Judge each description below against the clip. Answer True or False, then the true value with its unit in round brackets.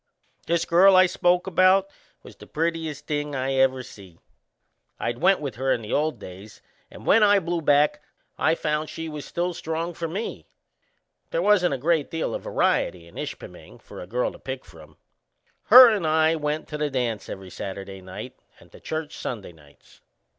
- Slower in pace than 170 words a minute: False (185 wpm)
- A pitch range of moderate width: False (5.9 semitones)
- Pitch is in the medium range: True (150 Hz)